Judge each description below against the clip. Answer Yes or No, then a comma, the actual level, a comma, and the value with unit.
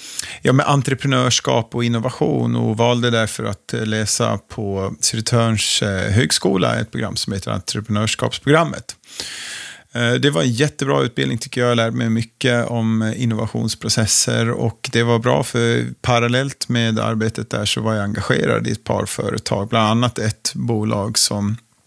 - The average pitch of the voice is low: Yes, low, 115 Hz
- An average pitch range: No, narrow, 1.8 semitones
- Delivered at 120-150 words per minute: Yes, average, 145 wpm